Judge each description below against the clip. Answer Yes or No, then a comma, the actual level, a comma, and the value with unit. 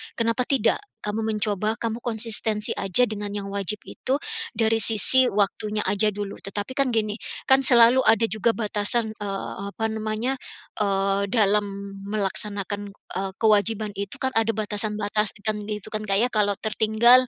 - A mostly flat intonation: Yes, narrow, 1.8 semitones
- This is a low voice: No, high, 215 Hz